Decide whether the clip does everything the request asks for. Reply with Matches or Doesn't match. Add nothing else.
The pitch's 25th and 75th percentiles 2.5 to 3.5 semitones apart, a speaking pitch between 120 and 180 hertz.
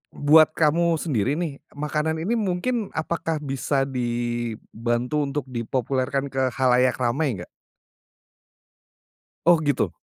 Doesn't match